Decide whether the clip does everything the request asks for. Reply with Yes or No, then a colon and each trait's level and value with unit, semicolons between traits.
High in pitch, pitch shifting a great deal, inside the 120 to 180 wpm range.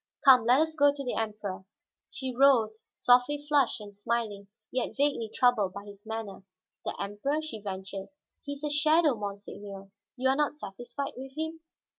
Yes: high, 245 Hz; wide, 5.7 semitones; average, 170 wpm